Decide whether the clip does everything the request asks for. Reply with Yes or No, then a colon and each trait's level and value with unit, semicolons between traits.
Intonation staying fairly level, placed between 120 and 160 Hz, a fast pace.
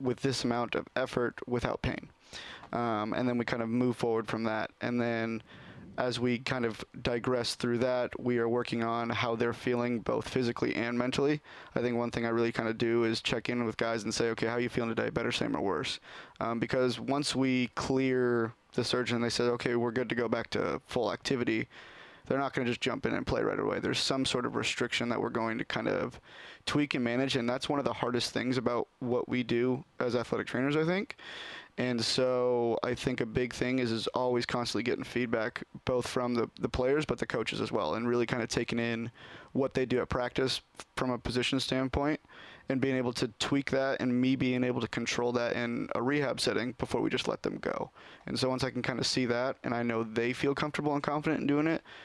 Yes: narrow, 1.6 semitones; low, 125 Hz; fast, 235 wpm